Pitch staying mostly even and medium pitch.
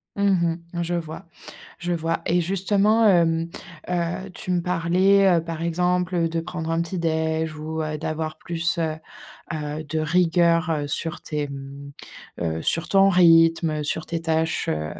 Yes: narrow, 1.9 semitones; medium, 165 Hz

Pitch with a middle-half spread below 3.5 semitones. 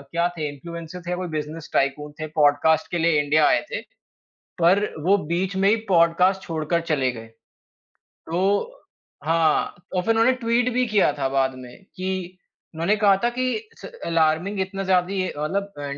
No: average, 3.8 semitones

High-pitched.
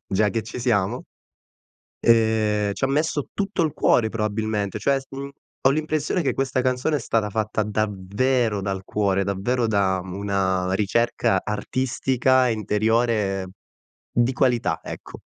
No: low, 110 Hz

